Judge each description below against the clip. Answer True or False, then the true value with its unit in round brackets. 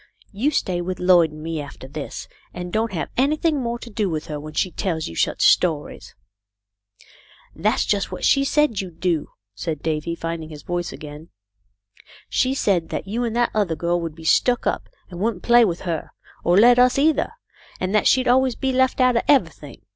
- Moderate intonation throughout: False (6.9 semitones)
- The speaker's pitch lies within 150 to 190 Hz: True (185 Hz)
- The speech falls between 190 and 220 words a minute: True (200 wpm)